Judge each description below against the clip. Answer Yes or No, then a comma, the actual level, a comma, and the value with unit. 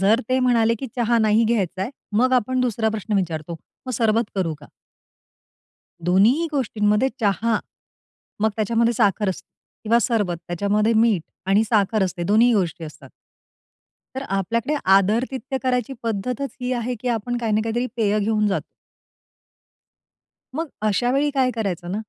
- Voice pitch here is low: No, high, 220 Hz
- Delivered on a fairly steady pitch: No, average, 3.4 semitones